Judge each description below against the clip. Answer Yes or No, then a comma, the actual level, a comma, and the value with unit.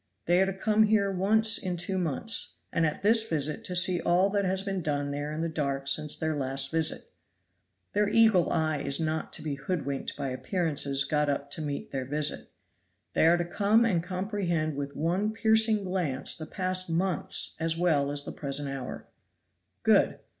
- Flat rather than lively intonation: No, average, 4.9 semitones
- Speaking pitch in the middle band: Yes, medium, 165 Hz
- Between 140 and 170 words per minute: No, average, 190 wpm